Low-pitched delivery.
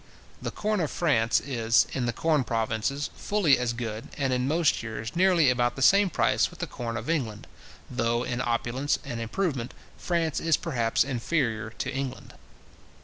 Yes: low, 125 Hz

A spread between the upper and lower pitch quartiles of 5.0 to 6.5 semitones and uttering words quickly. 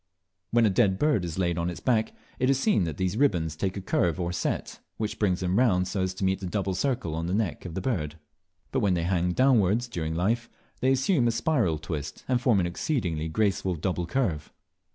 Yes: average, 5.3 semitones; fast, 230 wpm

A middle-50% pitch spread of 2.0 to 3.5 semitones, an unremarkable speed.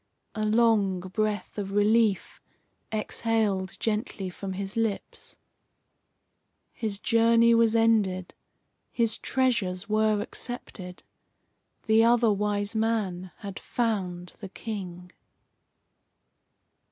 No: average, 2.8 semitones; slow, 90 wpm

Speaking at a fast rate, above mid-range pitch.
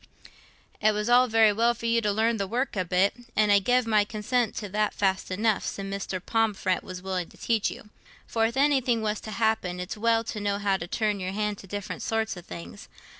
Yes: fast, 225 wpm; high, 210 Hz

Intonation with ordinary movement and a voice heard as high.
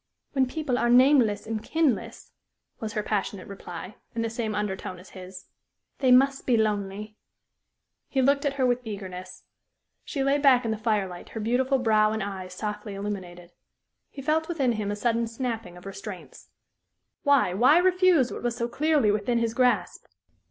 Yes: average, 4.3 semitones; high, 225 Hz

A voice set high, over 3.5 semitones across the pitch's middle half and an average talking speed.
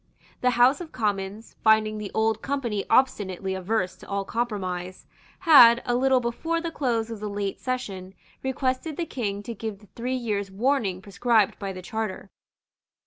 Yes: high, 220 Hz; average, 4.1 semitones; average, 165 wpm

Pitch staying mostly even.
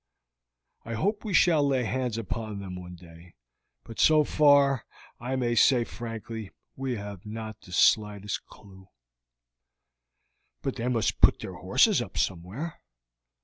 No: average, 4.7 semitones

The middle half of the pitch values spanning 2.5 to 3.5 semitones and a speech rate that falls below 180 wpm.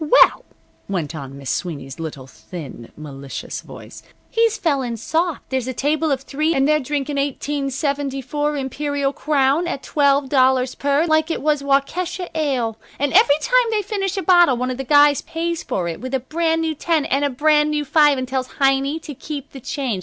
No: average, 3.2 semitones; average, 190 wpm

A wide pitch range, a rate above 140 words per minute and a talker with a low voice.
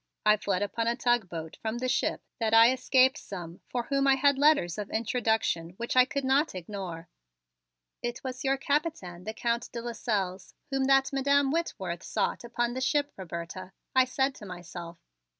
No: wide, 6.0 semitones; average, 180 wpm; high, 235 Hz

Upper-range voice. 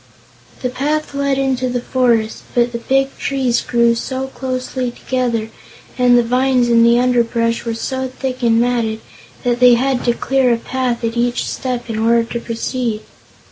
Yes: high, 245 Hz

